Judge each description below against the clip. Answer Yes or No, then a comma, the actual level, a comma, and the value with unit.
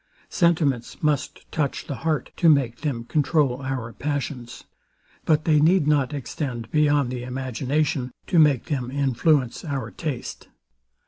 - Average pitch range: Yes, average, 3.2 semitones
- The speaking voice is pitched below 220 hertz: Yes, medium, 140 Hz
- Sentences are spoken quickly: No, slow, 135 wpm